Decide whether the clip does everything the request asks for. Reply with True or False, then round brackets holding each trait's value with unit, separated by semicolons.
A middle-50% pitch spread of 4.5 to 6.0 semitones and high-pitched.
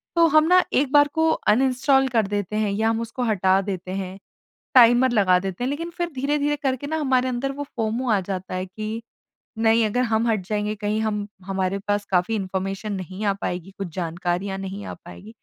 True (4.9 semitones; 215 Hz)